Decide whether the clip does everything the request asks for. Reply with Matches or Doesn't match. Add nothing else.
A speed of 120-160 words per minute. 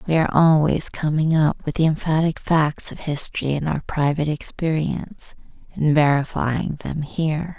Matches